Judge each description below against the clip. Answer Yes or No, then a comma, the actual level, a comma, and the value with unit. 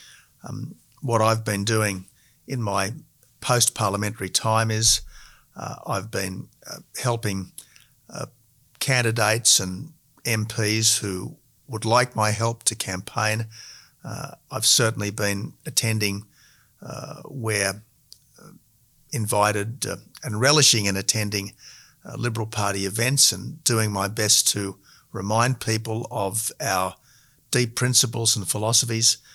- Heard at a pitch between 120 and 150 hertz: No, low, 110 Hz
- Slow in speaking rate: Yes, slow, 120 wpm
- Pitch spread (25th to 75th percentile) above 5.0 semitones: No, average, 3.0 semitones